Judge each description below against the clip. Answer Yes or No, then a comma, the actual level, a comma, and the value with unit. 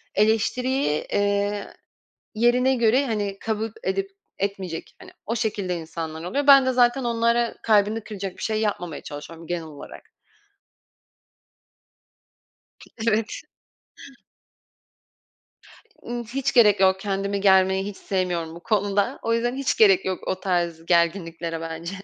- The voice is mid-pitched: No, high, 200 Hz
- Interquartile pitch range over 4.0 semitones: Yes, average, 4.4 semitones